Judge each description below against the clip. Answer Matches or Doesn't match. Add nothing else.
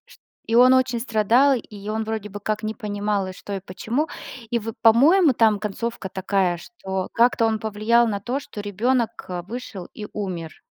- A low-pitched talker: Doesn't match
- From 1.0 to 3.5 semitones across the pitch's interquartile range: Matches